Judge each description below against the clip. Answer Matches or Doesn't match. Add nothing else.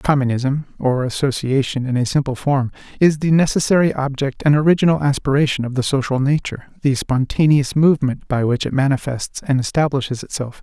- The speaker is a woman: Doesn't match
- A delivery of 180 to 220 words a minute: Doesn't match